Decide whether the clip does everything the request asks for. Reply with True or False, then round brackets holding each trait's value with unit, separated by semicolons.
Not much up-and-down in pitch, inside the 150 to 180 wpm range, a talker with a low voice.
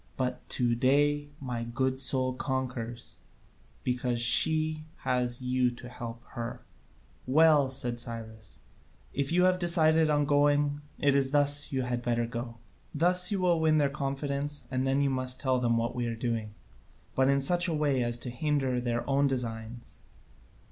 False (3.3 semitones; 165 wpm; 130 Hz)